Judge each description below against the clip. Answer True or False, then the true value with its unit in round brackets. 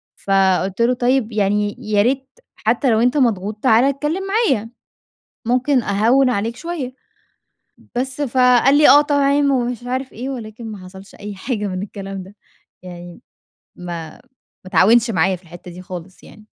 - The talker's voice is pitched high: True (225 Hz)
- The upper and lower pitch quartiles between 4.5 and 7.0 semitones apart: True (5.0 semitones)